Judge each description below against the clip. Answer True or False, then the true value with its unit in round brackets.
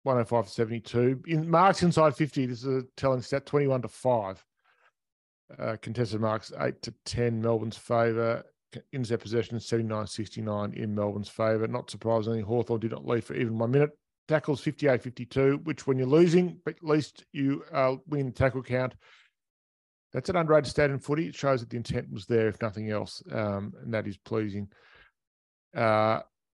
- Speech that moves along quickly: False (175 wpm)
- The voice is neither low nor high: False (120 Hz)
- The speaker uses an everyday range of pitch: True (3.9 semitones)